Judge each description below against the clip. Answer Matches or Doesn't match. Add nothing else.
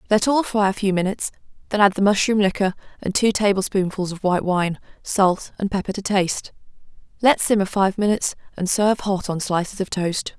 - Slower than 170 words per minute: Doesn't match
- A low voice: Doesn't match